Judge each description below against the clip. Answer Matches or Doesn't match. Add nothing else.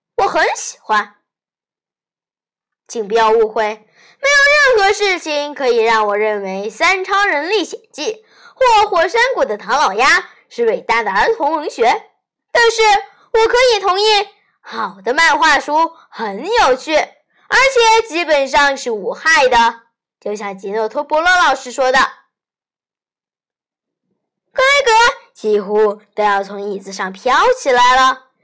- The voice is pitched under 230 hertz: Doesn't match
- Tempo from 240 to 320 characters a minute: Doesn't match